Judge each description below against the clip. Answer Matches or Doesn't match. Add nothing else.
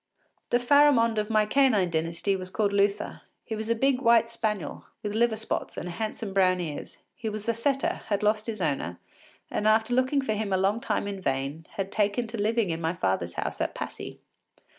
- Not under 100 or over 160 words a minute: Doesn't match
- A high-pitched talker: Matches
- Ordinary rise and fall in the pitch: Matches